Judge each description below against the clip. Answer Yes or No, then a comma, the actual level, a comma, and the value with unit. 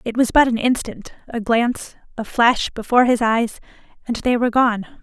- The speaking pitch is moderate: No, high, 235 Hz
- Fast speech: No, average, 190 wpm